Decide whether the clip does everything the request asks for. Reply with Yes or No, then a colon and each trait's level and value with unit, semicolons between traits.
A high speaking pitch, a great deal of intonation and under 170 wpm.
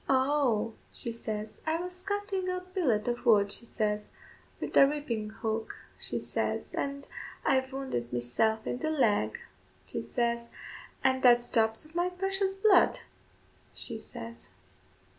Yes: high, 245 Hz; wide, 6.4 semitones; average, 140 wpm